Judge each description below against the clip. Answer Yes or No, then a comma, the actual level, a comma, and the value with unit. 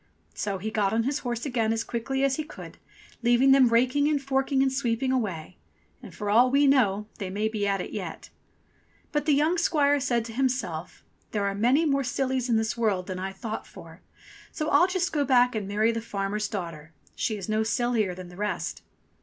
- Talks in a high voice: Yes, high, 235 Hz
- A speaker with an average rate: No, fast, 210 wpm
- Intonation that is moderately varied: Yes, average, 4.6 semitones